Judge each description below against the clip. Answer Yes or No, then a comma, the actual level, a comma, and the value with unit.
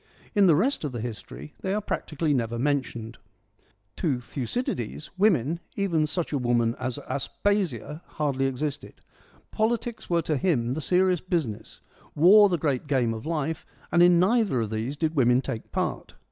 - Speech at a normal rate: Yes, average, 160 wpm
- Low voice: No, medium, 150 Hz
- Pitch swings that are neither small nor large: No, wide, 6.5 semitones